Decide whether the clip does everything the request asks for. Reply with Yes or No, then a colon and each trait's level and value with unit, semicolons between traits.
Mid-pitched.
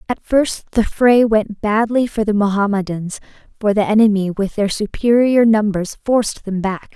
No: high, 210 Hz